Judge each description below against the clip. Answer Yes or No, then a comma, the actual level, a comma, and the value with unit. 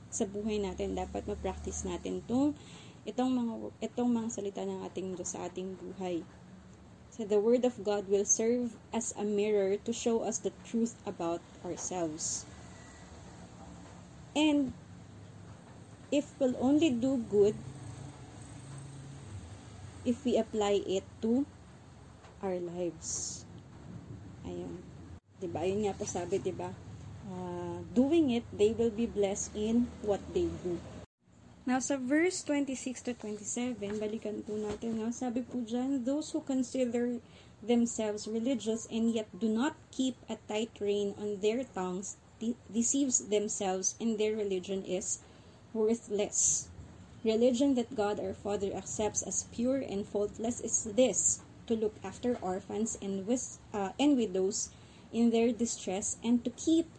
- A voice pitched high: Yes, high, 215 Hz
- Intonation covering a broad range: No, average, 4.1 semitones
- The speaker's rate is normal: Yes, average, 140 wpm